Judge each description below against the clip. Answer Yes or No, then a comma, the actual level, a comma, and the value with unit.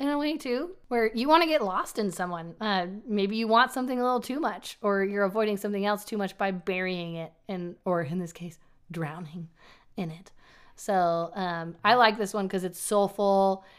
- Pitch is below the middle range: No, high, 200 Hz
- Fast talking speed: Yes, fast, 210 wpm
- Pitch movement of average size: Yes, average, 3.9 semitones